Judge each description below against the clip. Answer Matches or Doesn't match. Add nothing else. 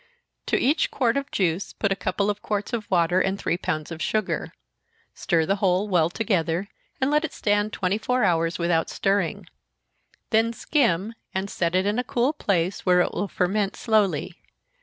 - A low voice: Doesn't match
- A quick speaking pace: Doesn't match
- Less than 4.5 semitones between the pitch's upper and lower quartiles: Matches